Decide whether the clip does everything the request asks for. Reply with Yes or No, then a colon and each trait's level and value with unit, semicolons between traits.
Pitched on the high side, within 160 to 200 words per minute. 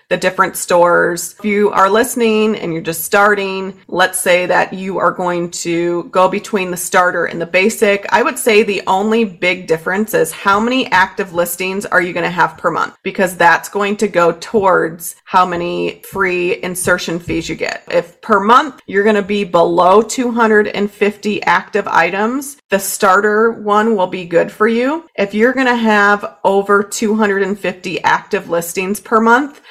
Yes: high, 195 Hz; average, 175 wpm